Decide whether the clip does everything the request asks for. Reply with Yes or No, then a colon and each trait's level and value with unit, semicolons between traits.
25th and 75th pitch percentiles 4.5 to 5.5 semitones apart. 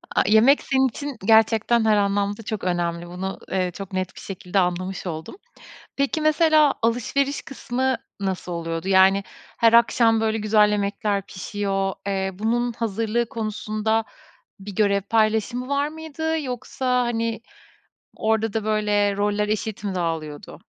No: average, 3.3 semitones